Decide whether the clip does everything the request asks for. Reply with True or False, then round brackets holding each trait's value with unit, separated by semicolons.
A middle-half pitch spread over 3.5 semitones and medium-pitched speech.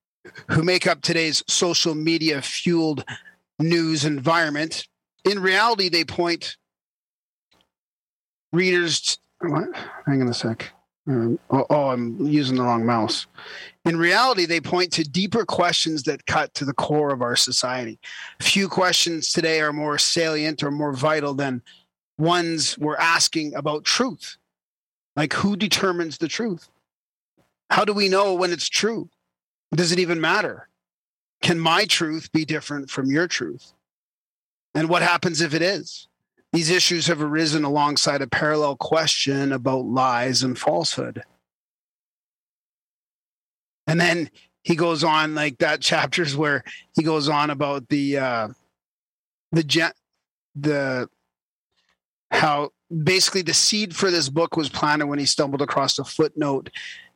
True (4.0 semitones; 155 Hz)